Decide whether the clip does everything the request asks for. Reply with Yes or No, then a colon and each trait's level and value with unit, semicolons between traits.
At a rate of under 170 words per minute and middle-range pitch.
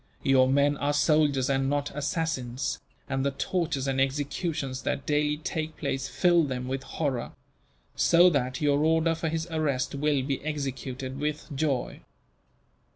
Yes: average, 150 wpm; medium, 145 Hz